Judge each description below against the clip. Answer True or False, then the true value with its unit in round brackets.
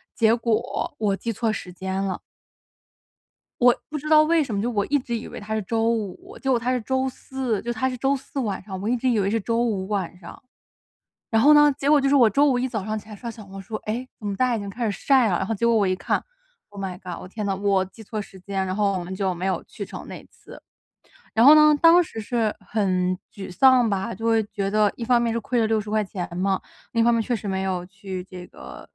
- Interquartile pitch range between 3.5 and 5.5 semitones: True (4.0 semitones)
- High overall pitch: True (220 Hz)